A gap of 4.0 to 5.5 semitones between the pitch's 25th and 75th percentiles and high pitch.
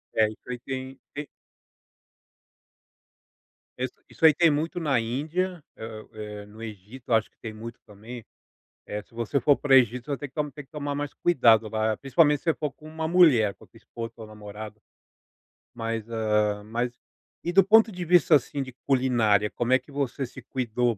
No: average, 4.8 semitones; low, 125 Hz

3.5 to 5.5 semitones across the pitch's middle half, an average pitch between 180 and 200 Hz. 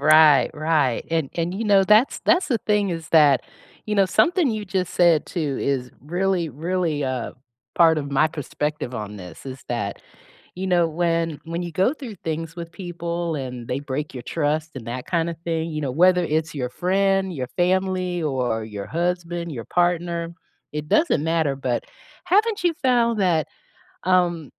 No: average, 4.0 semitones; medium, 165 Hz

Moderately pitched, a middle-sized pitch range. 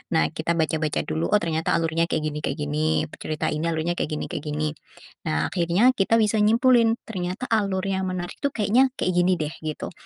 Yes: medium, 170 Hz; average, 4.7 semitones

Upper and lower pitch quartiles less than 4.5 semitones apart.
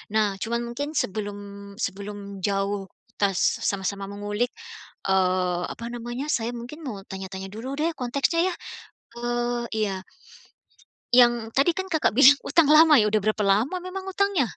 No: wide, 5.6 semitones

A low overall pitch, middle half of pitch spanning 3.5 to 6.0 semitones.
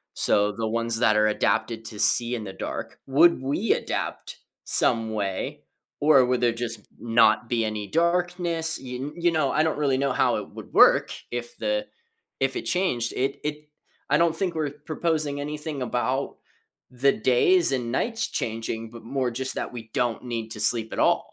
Yes: low, 125 Hz; average, 5.3 semitones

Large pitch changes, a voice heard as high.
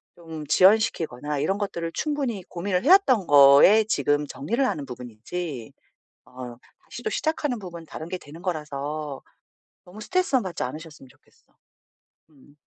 No: wide, 6.6 semitones; medium, 165 Hz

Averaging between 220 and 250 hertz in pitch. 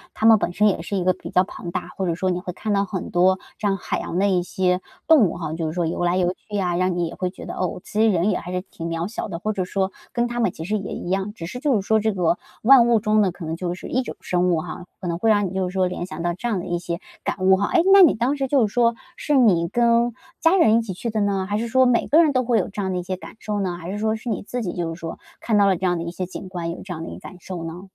No: high, 190 Hz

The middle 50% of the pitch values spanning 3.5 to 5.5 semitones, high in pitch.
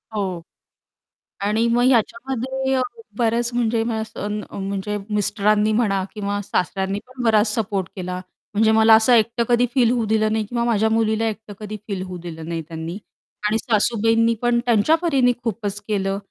No: narrow, 2.5 semitones; high, 220 Hz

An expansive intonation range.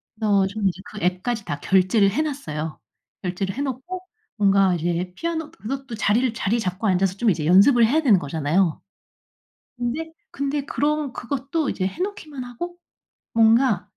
Yes: wide, 6.7 semitones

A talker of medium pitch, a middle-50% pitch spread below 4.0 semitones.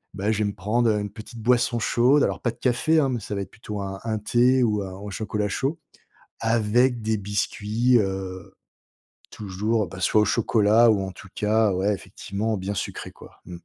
No: low, 105 Hz; average, 2.8 semitones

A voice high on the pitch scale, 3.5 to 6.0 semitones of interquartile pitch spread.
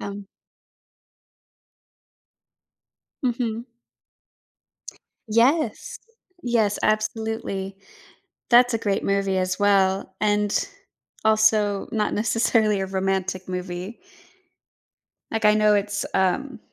No: high, 210 Hz; narrow, 2.5 semitones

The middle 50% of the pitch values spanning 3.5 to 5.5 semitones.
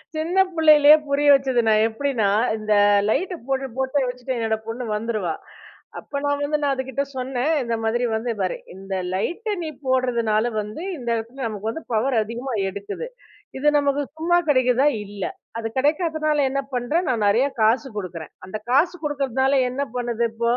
Yes: average, 4.2 semitones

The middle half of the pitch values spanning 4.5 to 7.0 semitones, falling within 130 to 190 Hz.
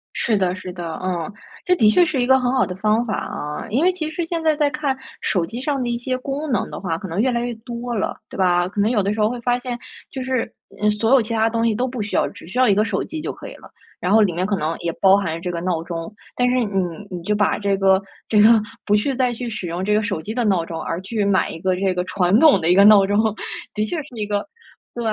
No: average, 4.8 semitones; high, 210 Hz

